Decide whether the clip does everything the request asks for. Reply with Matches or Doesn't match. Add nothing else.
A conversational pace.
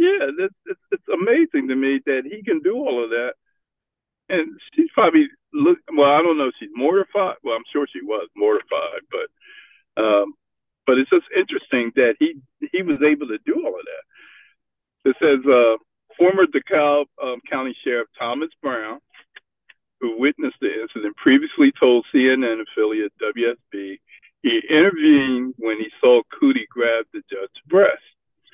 Matches